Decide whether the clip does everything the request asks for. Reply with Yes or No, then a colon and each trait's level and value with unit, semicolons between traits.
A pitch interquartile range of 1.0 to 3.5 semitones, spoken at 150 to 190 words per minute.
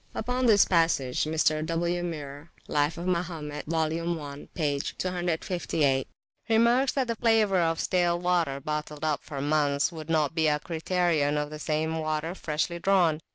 Yes: average, 2.8 semitones; average, 155 wpm